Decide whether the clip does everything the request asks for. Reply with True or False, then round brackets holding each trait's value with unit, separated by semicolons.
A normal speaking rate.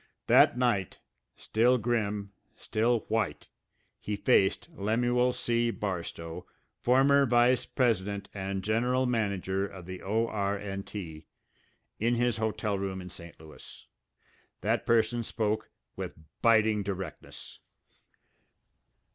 False (105 wpm)